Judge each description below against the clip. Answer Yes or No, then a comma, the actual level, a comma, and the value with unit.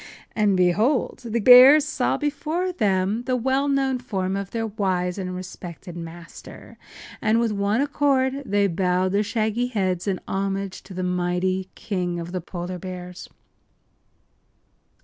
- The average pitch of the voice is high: Yes, high, 200 Hz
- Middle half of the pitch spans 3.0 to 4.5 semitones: No, average, 5.3 semitones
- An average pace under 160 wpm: Yes, average, 145 wpm